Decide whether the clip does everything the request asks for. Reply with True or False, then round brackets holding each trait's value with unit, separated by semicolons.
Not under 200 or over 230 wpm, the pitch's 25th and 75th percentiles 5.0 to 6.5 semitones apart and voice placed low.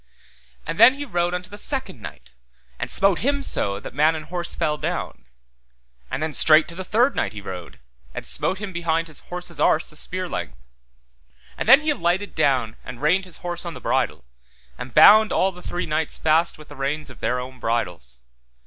False (205 wpm; 5.4 semitones; 165 Hz)